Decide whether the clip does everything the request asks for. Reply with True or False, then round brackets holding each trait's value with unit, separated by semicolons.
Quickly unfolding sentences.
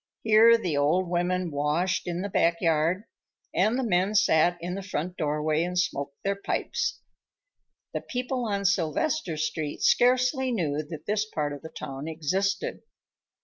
False (155 wpm)